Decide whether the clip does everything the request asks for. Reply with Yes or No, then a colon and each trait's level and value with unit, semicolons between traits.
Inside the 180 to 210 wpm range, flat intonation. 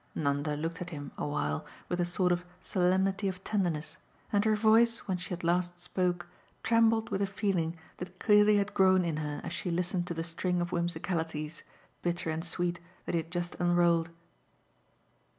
Yes: average, 185 wpm; narrow, 2.3 semitones